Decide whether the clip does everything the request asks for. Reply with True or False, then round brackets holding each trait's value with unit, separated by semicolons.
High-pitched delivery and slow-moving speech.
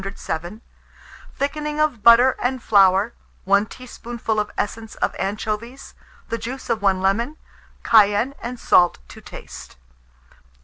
True (225 Hz; 125 wpm)